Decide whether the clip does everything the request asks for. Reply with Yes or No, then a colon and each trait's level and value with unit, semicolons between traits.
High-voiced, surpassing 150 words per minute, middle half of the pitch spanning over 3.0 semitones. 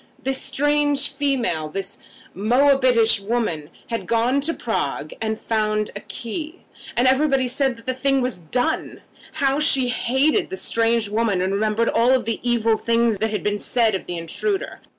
Yes: high, 235 Hz; average, 170 wpm; average, 3.9 semitones